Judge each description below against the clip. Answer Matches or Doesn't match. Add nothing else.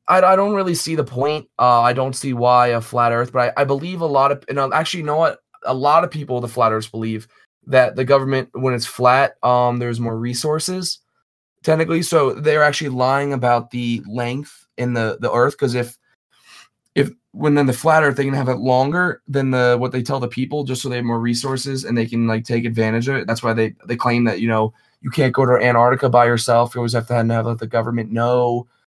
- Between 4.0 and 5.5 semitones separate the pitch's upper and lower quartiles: Doesn't match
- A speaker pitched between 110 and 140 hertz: Matches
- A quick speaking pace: Matches